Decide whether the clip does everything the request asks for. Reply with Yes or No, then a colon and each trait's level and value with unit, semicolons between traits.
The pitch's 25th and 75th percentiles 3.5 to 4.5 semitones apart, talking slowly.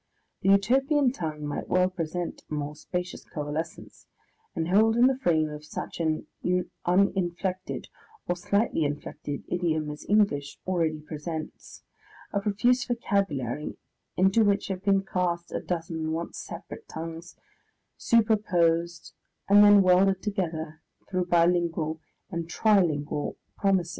Yes: average, 3.9 semitones; slow, 125 wpm